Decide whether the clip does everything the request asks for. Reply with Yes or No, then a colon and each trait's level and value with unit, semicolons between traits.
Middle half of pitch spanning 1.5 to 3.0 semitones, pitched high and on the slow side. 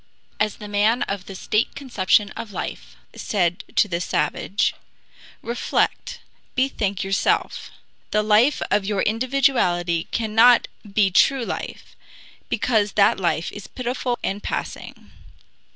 No: average, 3.5 semitones; high, 210 Hz; slow, 120 wpm